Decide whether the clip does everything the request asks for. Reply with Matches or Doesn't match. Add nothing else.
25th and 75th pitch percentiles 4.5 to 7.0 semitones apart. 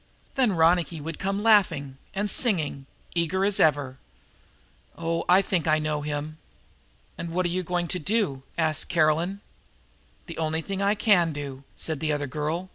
Doesn't match